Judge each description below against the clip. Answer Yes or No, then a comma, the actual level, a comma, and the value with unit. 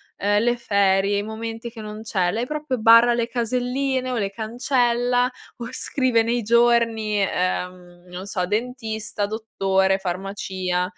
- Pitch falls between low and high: No, high, 220 Hz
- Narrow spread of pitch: No, average, 3.6 semitones